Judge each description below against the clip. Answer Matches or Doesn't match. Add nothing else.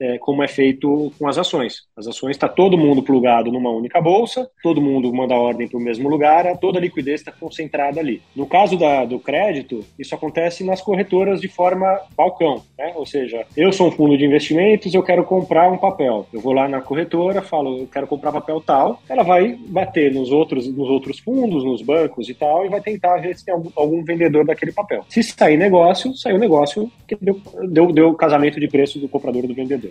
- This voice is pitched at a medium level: Matches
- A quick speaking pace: Matches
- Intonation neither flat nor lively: Matches